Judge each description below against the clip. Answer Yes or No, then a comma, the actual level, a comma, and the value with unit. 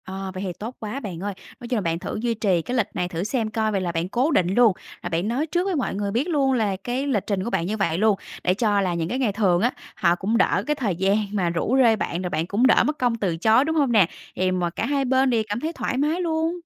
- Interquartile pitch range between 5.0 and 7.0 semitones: Yes, wide, 5.5 semitones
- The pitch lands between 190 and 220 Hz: Yes, high, 215 Hz